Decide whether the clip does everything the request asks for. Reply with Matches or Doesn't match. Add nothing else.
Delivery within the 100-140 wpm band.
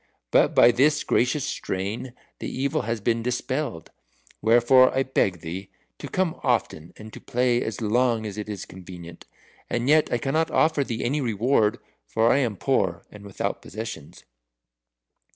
Doesn't match